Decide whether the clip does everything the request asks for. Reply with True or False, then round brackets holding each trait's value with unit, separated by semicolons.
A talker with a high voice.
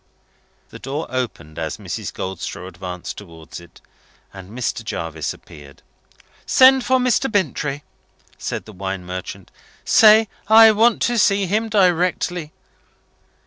False (135 Hz)